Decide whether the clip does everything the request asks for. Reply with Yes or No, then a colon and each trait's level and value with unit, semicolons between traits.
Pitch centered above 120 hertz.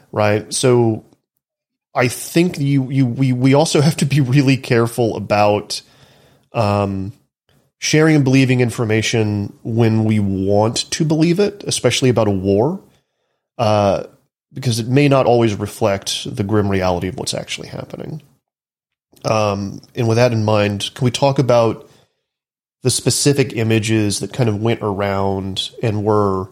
No: low, 115 Hz